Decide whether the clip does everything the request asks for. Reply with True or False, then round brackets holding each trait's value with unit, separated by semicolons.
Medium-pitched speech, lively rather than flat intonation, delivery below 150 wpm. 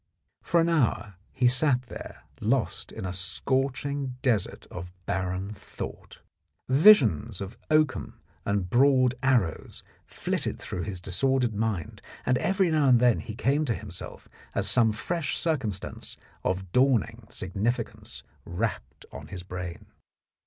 False (120 Hz; 6.1 semitones; 135 wpm)